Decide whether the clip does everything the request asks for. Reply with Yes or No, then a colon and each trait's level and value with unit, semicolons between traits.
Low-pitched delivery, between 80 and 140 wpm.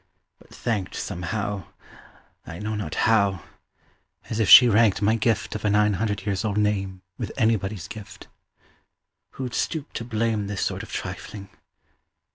No: low, 105 Hz; average, 150 wpm